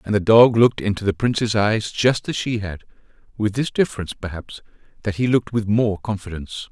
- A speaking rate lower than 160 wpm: No, average, 190 wpm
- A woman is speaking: No, male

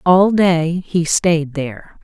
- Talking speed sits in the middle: Yes, average, 145 wpm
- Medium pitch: Yes, medium, 170 Hz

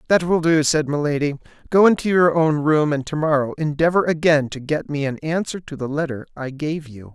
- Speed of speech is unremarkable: No, fast, 210 wpm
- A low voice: No, medium, 150 Hz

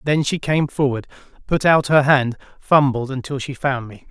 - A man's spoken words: Yes, male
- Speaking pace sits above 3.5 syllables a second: Yes, 4.8 syllables/s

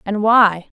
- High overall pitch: Yes, high, 205 Hz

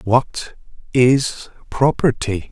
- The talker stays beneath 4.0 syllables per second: Yes, 2.7 syllables/s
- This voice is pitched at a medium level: No, low, 125 Hz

